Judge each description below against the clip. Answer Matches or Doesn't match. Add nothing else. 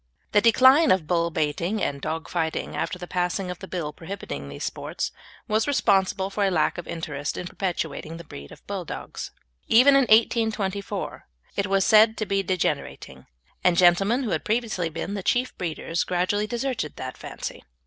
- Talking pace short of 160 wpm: Doesn't match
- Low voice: Doesn't match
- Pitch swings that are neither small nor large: Matches